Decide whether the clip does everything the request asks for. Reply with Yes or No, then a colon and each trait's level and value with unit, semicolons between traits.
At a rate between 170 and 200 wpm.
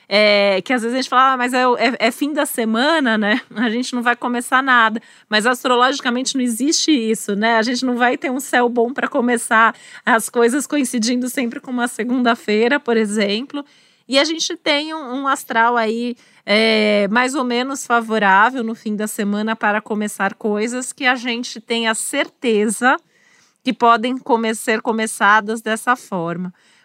Yes: average, 180 wpm